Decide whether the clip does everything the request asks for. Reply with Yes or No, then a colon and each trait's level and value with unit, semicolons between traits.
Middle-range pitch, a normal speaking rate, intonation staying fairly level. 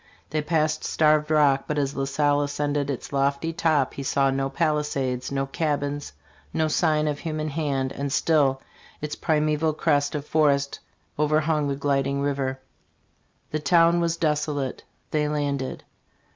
Yes: medium, 145 Hz; average, 160 wpm; narrow, 1.7 semitones